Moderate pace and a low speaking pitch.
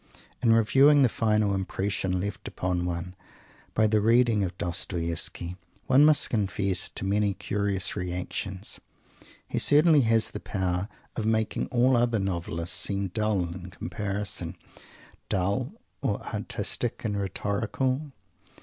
No: slow, 125 wpm; low, 100 Hz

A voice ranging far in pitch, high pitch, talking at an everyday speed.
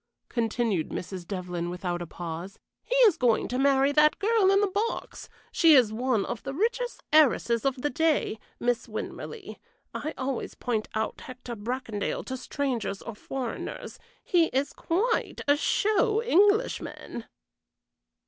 Yes: wide, 7.6 semitones; very high, 260 Hz; average, 145 wpm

